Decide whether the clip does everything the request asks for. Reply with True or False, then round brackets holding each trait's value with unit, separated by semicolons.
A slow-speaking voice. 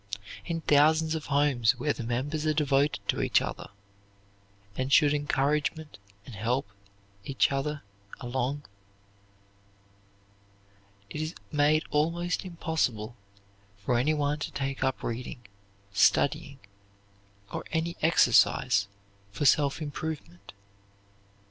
True (105 wpm)